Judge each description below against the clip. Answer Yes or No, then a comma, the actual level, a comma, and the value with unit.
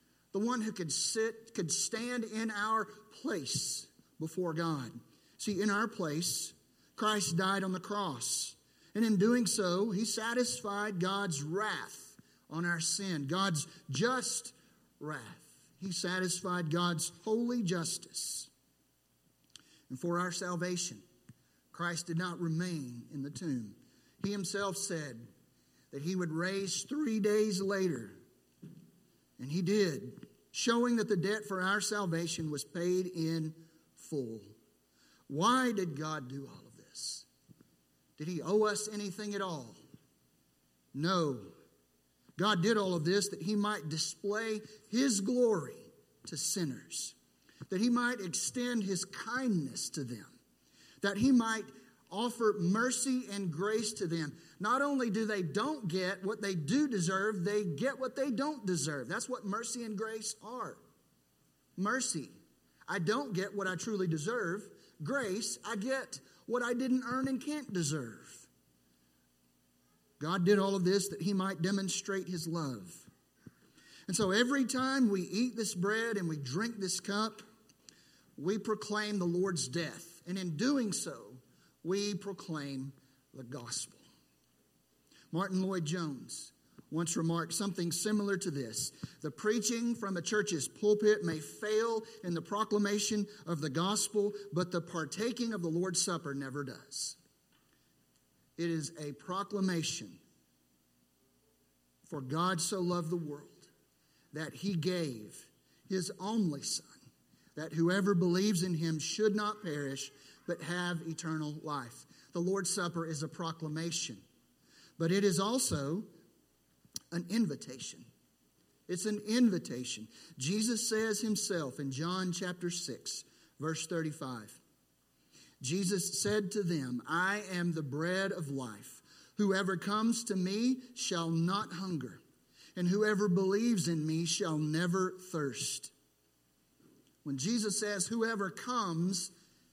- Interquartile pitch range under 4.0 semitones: No, average, 5.3 semitones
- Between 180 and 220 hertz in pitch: Yes, medium, 185 Hz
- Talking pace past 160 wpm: No, slow, 135 wpm